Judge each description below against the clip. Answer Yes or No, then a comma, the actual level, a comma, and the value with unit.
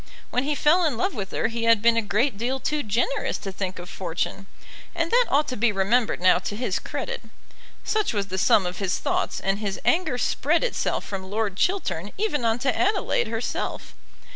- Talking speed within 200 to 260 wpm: Yes, fast, 205 wpm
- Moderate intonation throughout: No, wide, 7.0 semitones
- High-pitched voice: Yes, high, 230 Hz